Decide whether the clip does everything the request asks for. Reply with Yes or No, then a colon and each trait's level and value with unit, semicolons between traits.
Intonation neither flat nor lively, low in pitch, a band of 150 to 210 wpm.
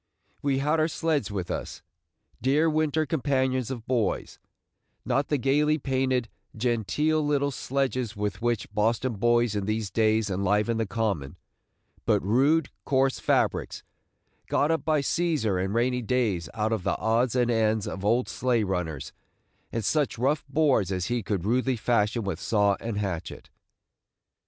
Yes: average, 4.6 semitones; low, 120 Hz; average, 155 wpm